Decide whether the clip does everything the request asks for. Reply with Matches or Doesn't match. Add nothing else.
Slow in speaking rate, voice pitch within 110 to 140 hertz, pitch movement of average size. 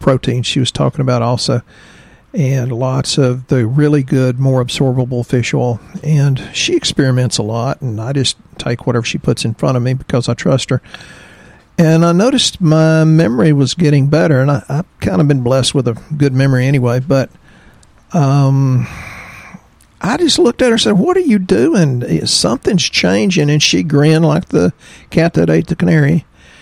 Doesn't match